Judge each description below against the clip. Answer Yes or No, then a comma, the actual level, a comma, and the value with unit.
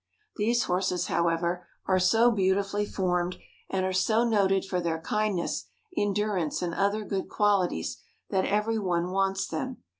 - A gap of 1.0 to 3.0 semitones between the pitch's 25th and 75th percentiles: Yes, narrow, 2.6 semitones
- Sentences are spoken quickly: No, average, 145 wpm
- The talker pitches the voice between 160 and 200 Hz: Yes, high, 190 Hz